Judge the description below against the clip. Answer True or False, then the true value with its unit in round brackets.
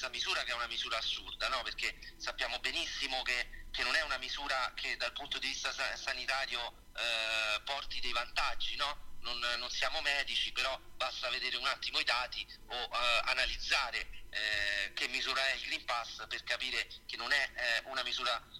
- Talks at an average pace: False (180 wpm)